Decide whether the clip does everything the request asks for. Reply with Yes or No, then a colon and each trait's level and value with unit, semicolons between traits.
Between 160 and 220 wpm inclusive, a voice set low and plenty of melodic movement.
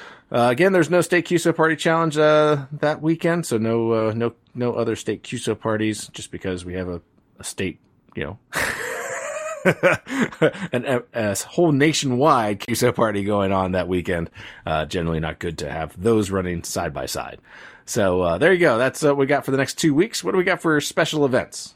Yes: average, 200 wpm; low, 125 Hz; wide, 8.1 semitones